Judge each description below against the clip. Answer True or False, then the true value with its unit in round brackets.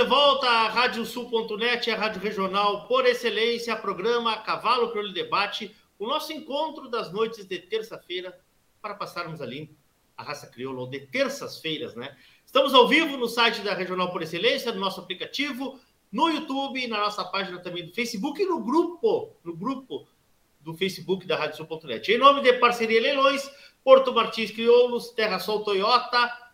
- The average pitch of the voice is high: True (230 Hz)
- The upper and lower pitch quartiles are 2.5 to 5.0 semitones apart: False (5.5 semitones)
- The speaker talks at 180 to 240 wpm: False (165 wpm)